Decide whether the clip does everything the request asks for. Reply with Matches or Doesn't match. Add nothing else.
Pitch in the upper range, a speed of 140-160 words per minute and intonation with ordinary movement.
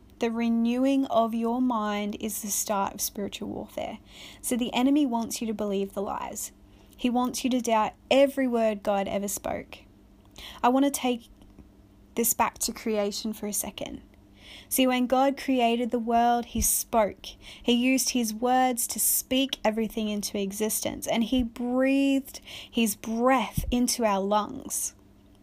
Matches